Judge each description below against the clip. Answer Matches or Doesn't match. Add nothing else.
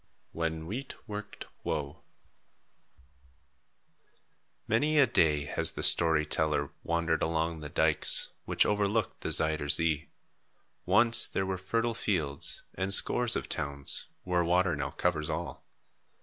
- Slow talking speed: Matches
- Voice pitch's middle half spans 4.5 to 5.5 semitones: Matches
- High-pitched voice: Doesn't match